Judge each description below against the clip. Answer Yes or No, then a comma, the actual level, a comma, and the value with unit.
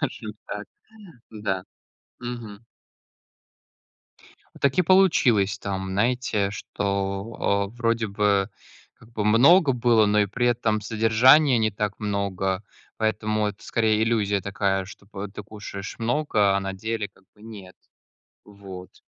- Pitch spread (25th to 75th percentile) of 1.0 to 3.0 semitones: Yes, narrow, 2.6 semitones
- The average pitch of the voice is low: Yes, low, 105 Hz